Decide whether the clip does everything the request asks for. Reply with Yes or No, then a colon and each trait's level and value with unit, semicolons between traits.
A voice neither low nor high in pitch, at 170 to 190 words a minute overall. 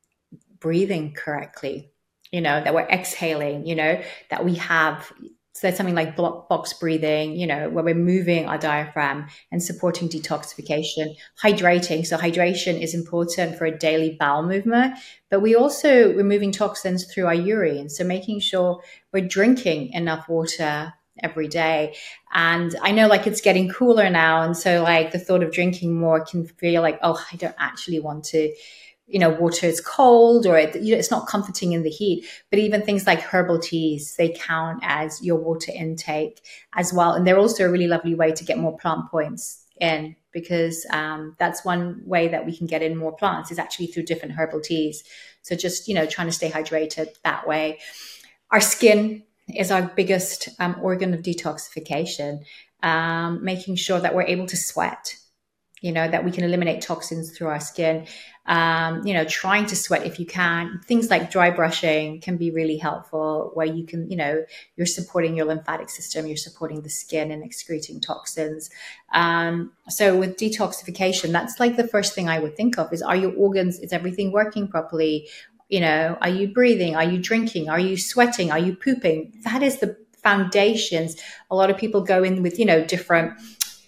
Yes: medium, 170 Hz; average, 185 wpm